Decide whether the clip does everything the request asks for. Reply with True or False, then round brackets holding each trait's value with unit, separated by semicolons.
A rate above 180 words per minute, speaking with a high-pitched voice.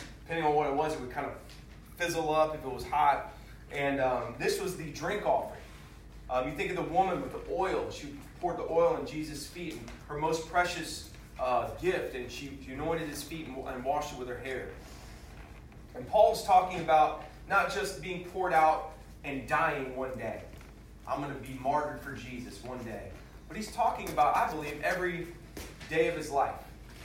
False (200 wpm; 150 Hz)